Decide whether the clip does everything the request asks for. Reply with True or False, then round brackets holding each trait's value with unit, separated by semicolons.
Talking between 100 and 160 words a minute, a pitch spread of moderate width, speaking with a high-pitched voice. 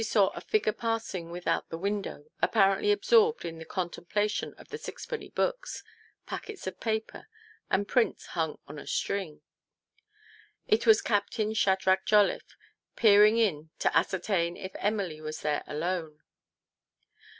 True (140 wpm; 4.3 semitones; 200 Hz)